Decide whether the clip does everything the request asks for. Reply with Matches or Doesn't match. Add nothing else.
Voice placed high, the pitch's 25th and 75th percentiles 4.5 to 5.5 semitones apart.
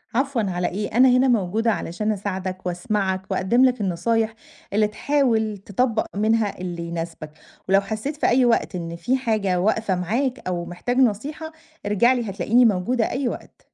Matches